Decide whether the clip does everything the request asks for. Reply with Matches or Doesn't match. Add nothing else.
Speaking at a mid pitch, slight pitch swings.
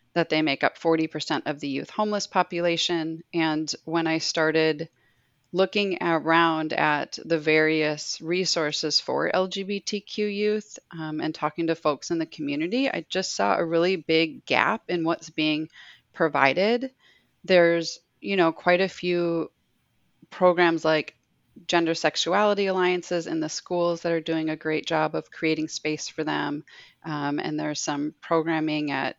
Matches